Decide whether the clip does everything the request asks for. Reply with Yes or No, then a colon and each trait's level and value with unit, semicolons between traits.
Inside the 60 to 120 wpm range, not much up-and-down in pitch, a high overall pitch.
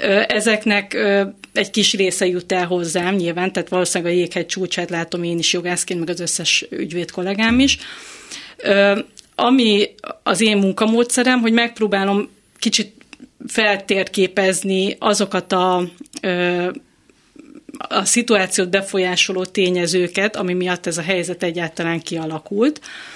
No: average, 115 wpm; average, 3.3 semitones; high, 195 Hz